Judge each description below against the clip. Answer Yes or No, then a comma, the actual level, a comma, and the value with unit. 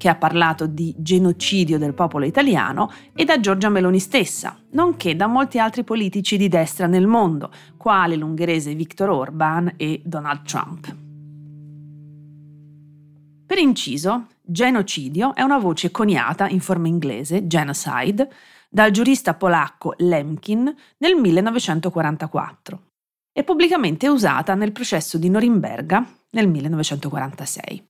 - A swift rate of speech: No, average, 120 wpm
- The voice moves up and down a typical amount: No, wide, 5.7 semitones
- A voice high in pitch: No, medium, 175 Hz